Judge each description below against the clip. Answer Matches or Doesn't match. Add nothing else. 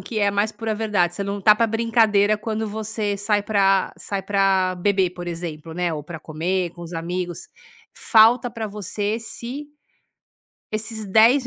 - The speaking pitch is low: Doesn't match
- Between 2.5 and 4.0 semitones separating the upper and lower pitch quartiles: Matches